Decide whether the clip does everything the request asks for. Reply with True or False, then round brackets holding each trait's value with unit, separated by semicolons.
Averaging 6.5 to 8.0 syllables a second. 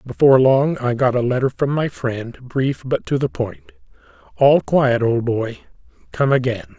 False (4.4 syllables/s)